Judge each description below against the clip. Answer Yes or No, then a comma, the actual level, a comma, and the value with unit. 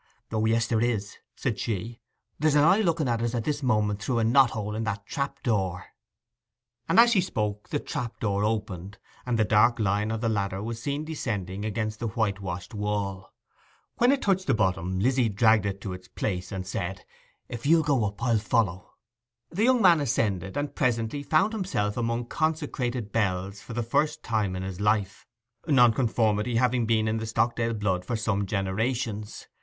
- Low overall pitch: Yes, low, 110 Hz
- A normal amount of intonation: Yes, average, 3.6 semitones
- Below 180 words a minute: No, average, 185 wpm